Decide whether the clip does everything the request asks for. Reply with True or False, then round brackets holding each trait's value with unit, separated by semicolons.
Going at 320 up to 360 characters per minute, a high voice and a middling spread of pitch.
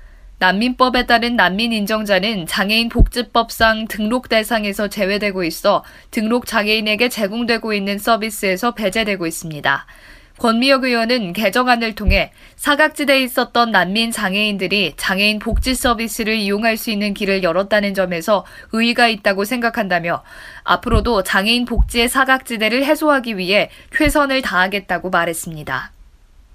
True (345 characters per minute; 220 Hz; 3.4 semitones)